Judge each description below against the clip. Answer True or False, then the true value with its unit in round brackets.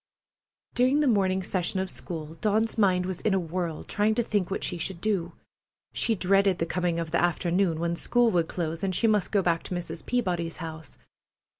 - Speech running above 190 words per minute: True (200 wpm)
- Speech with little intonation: False (3.3 semitones)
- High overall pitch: False (180 Hz)